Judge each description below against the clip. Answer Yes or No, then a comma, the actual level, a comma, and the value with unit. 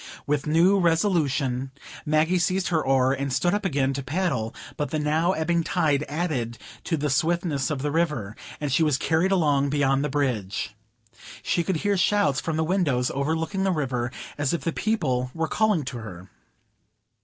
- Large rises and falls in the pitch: No, average, 4.2 semitones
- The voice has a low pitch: No, medium, 150 Hz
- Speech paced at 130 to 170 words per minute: No, average, 180 wpm